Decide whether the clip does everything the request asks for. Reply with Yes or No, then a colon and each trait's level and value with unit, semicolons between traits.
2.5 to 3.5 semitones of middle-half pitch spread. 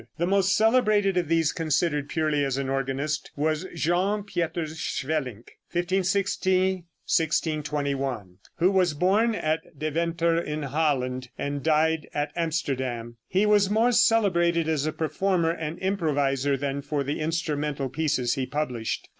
No: average, 3.9 semitones